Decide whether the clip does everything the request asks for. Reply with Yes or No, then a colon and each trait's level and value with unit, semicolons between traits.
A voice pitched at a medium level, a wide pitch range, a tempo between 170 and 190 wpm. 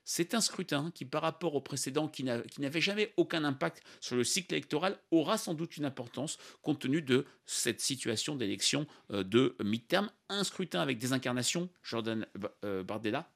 Yes: medium, 150 Hz; wide, 6.3 semitones; average, 185 wpm